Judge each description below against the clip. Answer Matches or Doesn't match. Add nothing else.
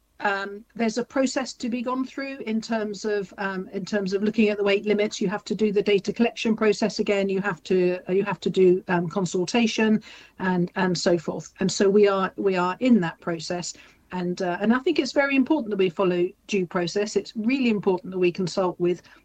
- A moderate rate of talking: Doesn't match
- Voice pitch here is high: Matches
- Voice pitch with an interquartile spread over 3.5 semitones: Doesn't match